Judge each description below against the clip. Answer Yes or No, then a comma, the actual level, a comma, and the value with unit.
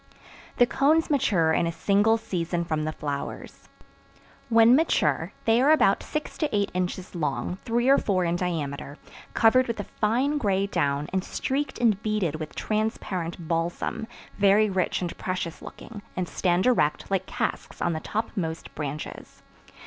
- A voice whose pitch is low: No, high, 190 Hz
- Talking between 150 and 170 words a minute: Yes, average, 155 wpm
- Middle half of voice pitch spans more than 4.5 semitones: Yes, average, 5.2 semitones